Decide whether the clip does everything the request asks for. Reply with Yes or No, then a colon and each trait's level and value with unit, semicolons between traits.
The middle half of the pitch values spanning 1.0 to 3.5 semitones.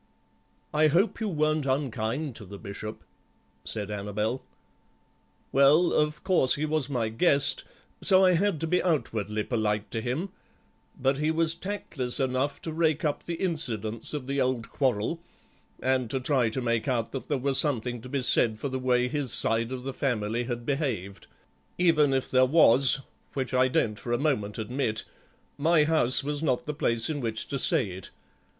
No: average, 4.6 semitones